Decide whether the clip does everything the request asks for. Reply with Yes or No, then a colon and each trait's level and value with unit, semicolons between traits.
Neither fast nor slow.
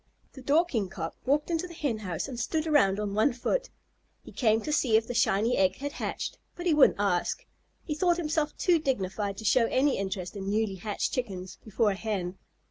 No: fast, 210 wpm